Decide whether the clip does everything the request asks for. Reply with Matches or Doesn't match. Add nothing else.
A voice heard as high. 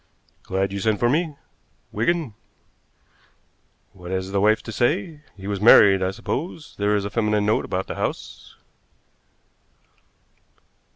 Doesn't match